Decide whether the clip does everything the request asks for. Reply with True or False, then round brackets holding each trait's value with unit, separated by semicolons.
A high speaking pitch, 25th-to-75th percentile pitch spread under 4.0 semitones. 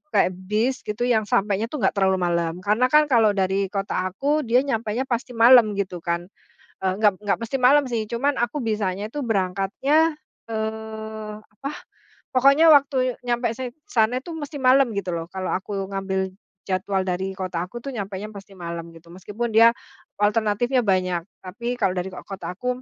False (215 Hz; 4.5 semitones)